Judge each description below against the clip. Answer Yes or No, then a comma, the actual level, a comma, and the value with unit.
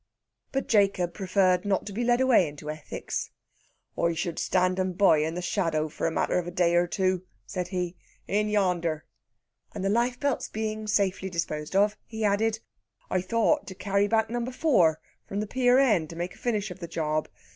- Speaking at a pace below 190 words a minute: No, average, 200 wpm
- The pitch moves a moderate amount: Yes, average, 3.8 semitones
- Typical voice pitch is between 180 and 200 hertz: Yes, high, 190 Hz